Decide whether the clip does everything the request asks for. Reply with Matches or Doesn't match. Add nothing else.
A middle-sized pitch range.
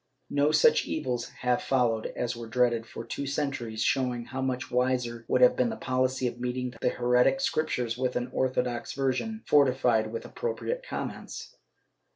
Doesn't match